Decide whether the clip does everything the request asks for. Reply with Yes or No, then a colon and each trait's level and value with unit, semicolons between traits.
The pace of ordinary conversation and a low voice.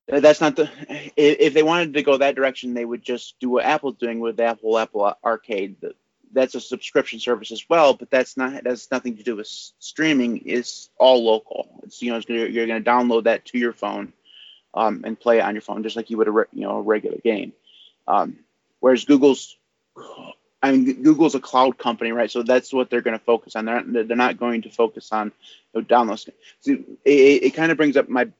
No: fast, 225 wpm; low, 120 Hz